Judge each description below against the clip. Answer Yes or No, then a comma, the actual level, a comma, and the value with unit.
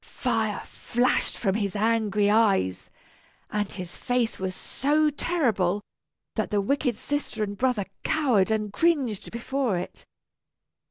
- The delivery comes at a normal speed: No, slow, 125 wpm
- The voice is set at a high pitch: Yes, high, 220 Hz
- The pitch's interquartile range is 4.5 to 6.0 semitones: No, average, 4.1 semitones